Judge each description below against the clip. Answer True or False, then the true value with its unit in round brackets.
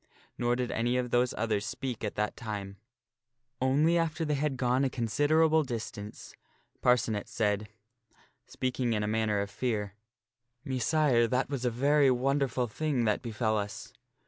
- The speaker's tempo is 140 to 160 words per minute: True (155 wpm)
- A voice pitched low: True (125 Hz)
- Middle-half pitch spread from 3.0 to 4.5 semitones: True (3.8 semitones)